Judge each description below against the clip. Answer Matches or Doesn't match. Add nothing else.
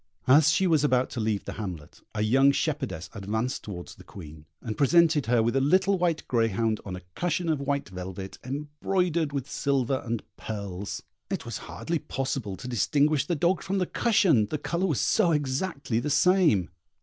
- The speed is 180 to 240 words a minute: Matches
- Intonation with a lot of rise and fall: Matches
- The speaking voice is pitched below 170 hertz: Matches